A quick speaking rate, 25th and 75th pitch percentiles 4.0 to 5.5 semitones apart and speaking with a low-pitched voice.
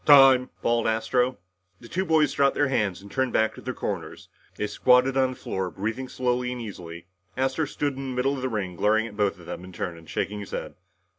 Yes: fast, 230 wpm; average, 4.4 semitones; low, 125 Hz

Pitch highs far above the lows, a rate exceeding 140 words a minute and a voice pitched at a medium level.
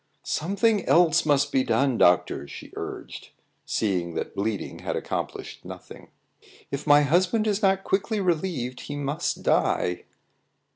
No: wide, 7.4 semitones; slow, 135 wpm; medium, 145 Hz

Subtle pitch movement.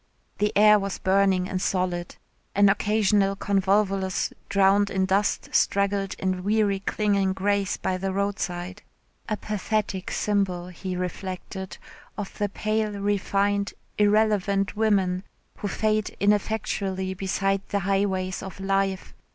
Yes: narrow, 1.4 semitones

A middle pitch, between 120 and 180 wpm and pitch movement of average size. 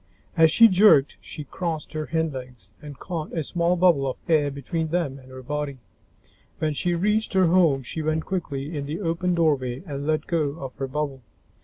No: medium, 155 Hz; average, 190 wpm; average, 3.5 semitones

